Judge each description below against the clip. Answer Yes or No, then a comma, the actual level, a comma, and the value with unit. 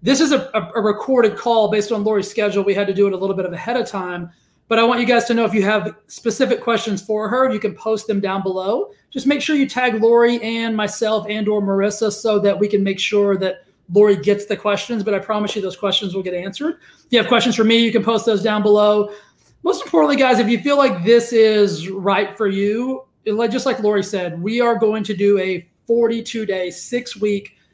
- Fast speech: Yes, fast, 240 wpm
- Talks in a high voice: Yes, high, 215 Hz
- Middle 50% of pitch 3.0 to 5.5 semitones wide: No, narrow, 2.6 semitones